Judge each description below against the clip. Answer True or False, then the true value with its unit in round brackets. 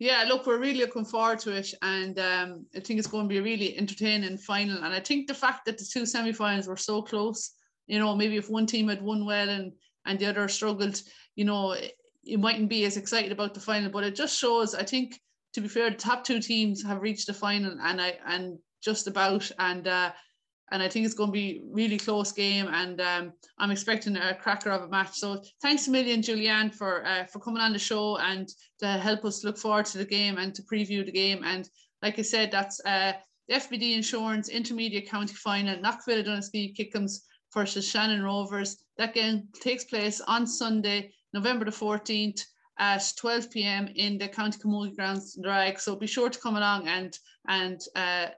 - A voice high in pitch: True (205 Hz)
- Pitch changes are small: True (2.1 semitones)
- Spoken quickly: True (210 wpm)